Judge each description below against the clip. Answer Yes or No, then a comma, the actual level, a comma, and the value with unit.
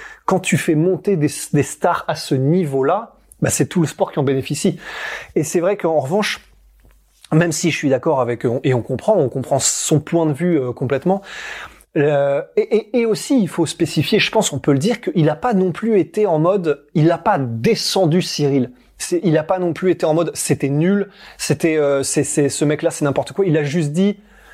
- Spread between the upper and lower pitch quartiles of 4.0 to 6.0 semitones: Yes, average, 4.6 semitones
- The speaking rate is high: Yes, fast, 225 wpm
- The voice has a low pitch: No, medium, 165 Hz